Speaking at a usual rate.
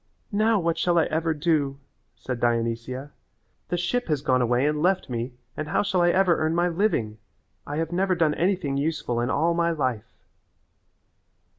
Yes: average, 175 wpm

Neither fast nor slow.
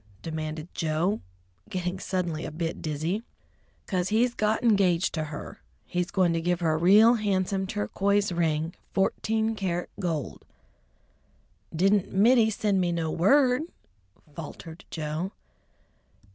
No: slow, 125 wpm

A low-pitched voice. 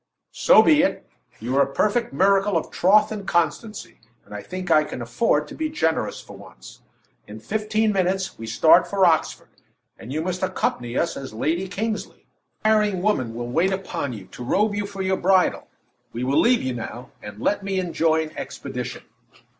No: medium, 180 Hz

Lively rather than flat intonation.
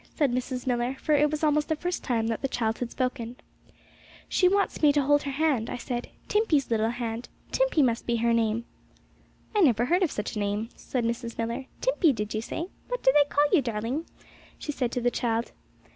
No: average, 4.3 semitones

